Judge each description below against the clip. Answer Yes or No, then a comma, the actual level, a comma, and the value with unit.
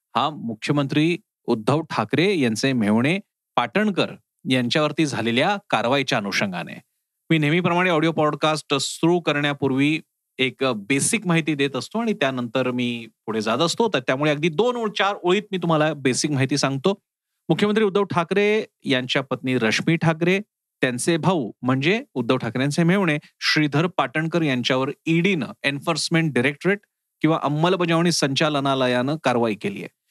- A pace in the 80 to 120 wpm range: No, fast, 130 wpm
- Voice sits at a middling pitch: Yes, medium, 155 Hz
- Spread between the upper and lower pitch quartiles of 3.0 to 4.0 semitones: No, average, 4.6 semitones